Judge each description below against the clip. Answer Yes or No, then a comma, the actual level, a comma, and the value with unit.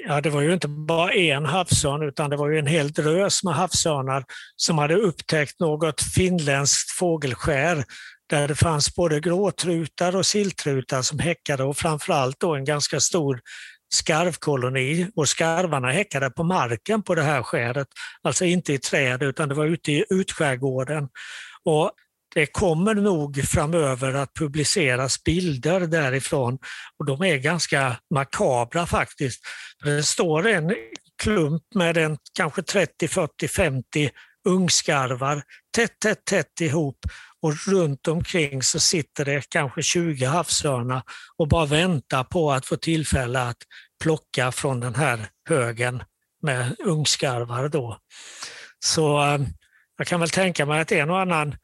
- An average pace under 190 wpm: Yes, average, 145 wpm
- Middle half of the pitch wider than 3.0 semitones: Yes, average, 3.9 semitones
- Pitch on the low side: No, medium, 155 Hz